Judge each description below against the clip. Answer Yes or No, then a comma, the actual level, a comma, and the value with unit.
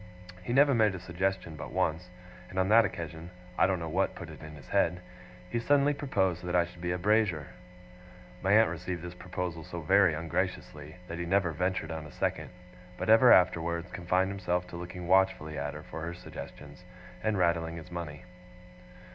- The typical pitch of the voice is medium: No, very low, 90 Hz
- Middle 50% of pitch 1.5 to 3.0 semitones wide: Yes, narrow, 2.4 semitones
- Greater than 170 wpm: Yes, average, 190 wpm